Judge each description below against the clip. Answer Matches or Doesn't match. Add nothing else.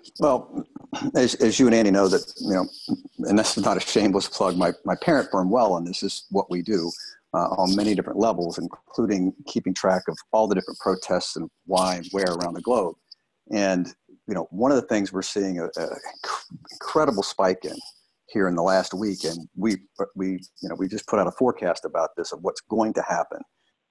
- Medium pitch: Doesn't match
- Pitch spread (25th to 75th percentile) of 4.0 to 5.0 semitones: Doesn't match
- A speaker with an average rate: Doesn't match